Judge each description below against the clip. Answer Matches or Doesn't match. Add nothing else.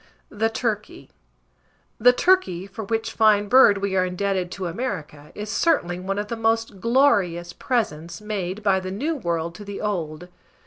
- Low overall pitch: Doesn't match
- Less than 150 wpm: Doesn't match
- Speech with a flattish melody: Doesn't match